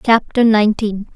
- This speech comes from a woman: Yes, female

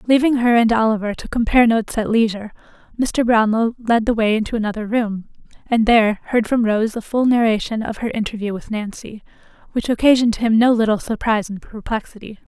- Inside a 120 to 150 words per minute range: No, average, 180 wpm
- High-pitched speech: Yes, high, 225 Hz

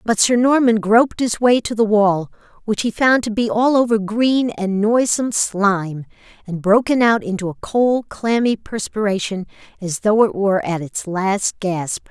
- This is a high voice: Yes, high, 210 Hz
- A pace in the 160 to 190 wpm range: Yes, average, 180 wpm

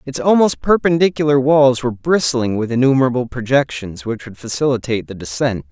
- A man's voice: Yes, male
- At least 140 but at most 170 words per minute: Yes, average, 145 wpm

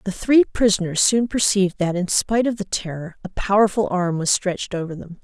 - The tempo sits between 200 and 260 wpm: Yes, fast, 205 wpm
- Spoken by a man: No, female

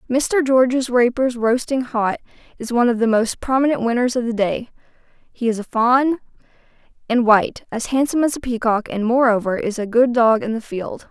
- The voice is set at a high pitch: Yes, high, 240 Hz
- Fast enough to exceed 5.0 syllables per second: Yes, 5.3 syllables/s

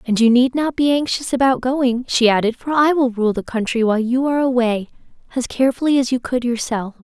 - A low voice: No, very high, 250 Hz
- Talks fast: Yes, fast, 220 wpm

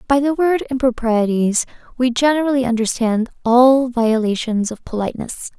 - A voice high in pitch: Yes, high, 245 Hz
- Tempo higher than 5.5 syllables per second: No, 4.9 syllables/s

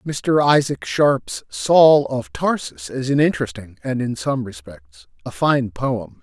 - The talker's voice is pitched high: No, low, 120 Hz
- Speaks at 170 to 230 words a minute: No, average, 155 wpm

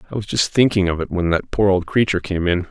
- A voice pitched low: Yes, very low, 95 Hz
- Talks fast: Yes, fast, 290 wpm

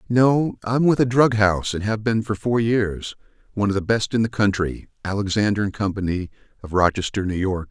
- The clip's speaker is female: No, male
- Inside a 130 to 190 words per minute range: No, average, 200 wpm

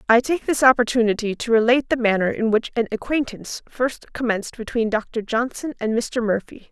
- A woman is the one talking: Yes, female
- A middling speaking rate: Yes, average, 180 wpm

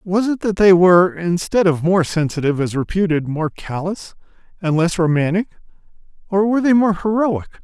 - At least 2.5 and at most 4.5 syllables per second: No, 5.4 syllables/s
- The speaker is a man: Yes, male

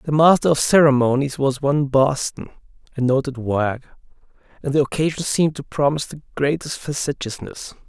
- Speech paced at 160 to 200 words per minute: No, average, 145 wpm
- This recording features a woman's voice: No, male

